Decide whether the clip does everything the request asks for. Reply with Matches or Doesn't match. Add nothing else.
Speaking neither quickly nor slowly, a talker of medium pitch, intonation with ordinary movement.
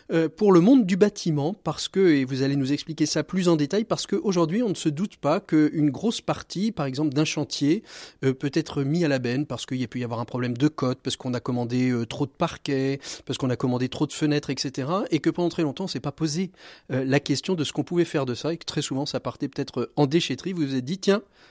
Doesn't match